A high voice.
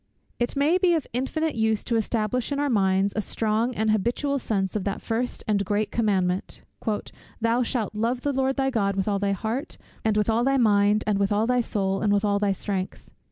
Yes: high, 220 Hz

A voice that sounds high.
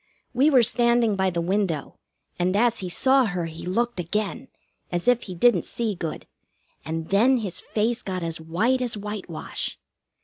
Yes: high, 205 Hz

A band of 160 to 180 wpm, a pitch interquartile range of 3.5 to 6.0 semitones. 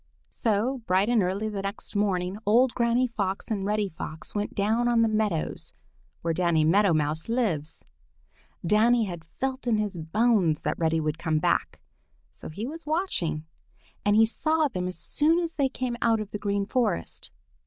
Yes: average, 175 wpm; average, 4.9 semitones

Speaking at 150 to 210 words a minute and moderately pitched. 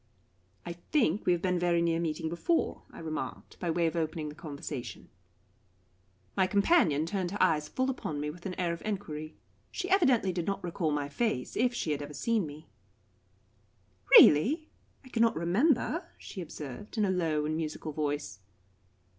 Yes: average, 170 wpm; medium, 170 Hz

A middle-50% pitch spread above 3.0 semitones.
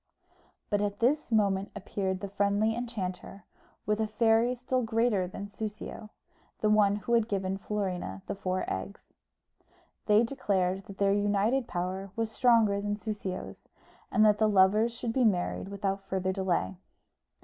No: narrow, 2.5 semitones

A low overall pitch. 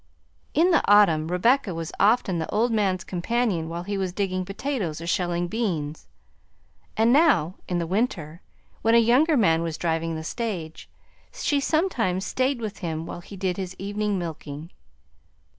No: high, 190 Hz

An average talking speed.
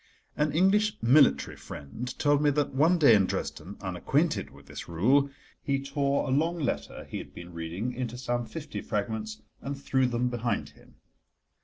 Yes: average, 170 wpm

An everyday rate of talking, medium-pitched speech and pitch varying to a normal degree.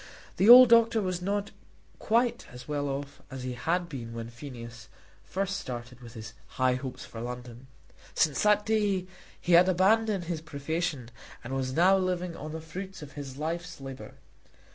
No: average, 170 wpm; medium, 155 Hz; wide, 6.6 semitones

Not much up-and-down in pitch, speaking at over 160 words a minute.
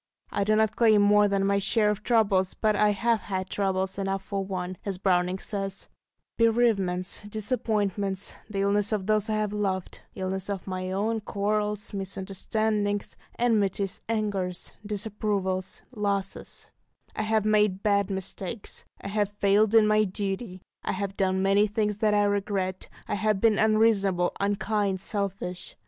No: narrow, 1.8 semitones; average, 150 wpm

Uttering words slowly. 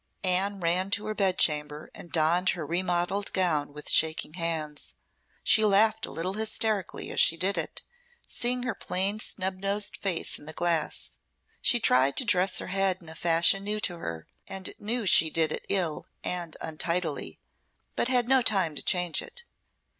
No: average, 175 wpm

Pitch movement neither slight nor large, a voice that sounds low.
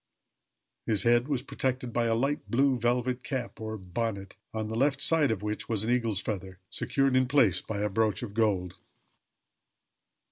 Yes: average, 3.4 semitones; low, 115 Hz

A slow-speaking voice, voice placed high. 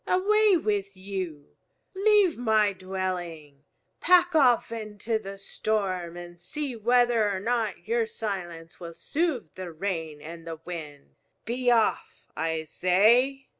Yes: slow, 130 wpm; high, 200 Hz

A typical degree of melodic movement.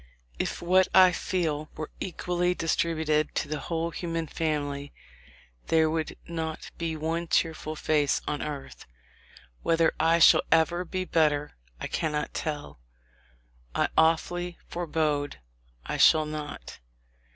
No: narrow, 1.8 semitones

